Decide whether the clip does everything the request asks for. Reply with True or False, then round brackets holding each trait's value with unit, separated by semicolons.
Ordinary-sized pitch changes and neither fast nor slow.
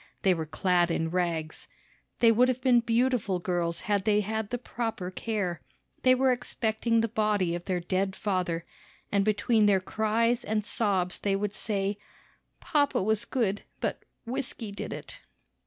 True (3.9 semitones; 160 wpm)